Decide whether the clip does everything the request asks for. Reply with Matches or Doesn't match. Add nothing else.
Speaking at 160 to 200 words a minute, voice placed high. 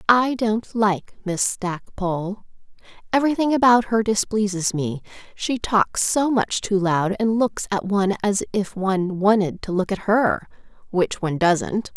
Doesn't match